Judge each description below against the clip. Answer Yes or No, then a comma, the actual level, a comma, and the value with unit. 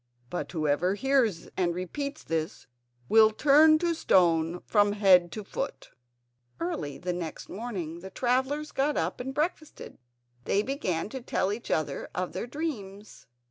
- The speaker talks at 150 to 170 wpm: No, average, 140 wpm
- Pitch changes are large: Yes, wide, 7.6 semitones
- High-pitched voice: Yes, high, 205 Hz